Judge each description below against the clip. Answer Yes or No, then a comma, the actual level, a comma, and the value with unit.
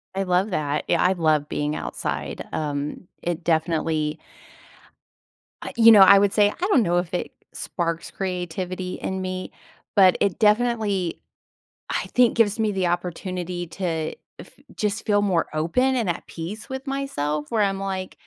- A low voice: No, medium, 185 Hz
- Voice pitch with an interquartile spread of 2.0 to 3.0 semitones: No, average, 3.7 semitones